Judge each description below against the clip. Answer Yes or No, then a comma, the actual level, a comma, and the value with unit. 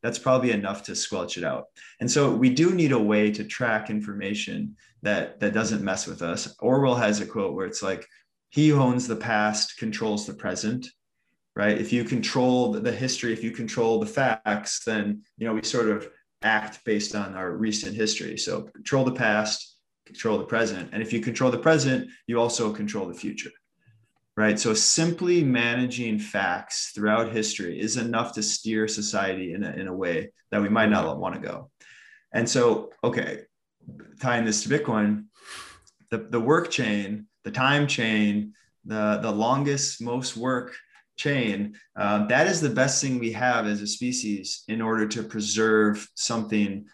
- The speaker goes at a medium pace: Yes, average, 175 wpm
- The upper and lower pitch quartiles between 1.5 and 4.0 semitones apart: Yes, average, 2.9 semitones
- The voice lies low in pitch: Yes, low, 110 Hz